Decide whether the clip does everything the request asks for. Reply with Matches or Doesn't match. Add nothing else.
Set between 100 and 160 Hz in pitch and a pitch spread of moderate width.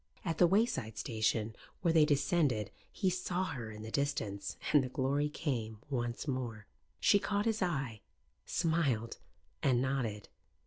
Doesn't match